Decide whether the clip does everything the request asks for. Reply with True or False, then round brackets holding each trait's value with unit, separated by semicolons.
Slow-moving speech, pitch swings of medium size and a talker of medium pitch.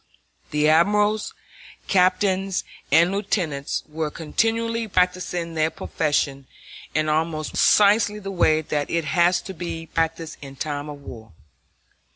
True (125 wpm; 3.9 semitones; 165 Hz)